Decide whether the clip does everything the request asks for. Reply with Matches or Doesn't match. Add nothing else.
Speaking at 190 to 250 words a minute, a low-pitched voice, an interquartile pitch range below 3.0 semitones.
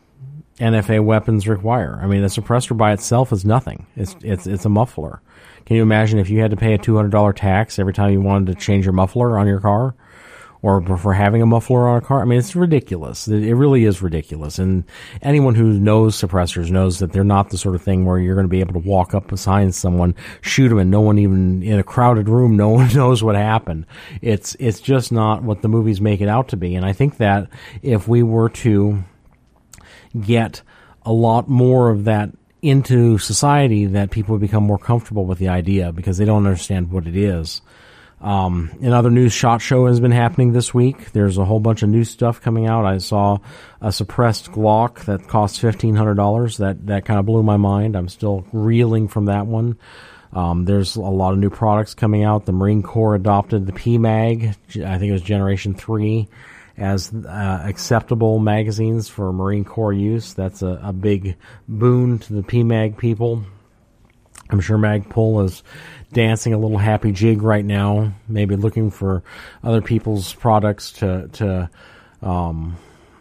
Matches